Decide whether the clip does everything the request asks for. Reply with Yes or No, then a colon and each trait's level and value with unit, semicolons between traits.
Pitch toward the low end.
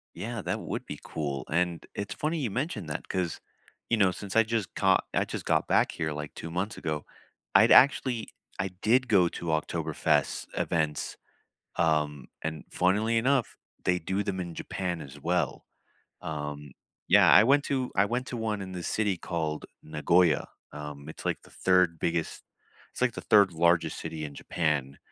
Yes: very low, 90 Hz